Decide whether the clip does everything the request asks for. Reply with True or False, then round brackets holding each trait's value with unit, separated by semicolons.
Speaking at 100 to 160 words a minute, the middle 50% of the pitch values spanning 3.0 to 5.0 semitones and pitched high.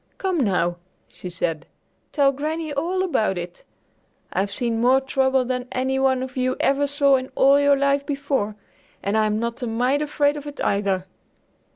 False (170 wpm; 4.5 semitones; 265 Hz)